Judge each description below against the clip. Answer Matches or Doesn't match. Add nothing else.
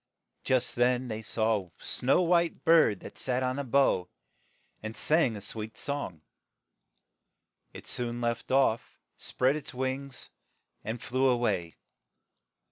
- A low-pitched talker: Matches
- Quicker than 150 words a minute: Doesn't match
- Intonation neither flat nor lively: Matches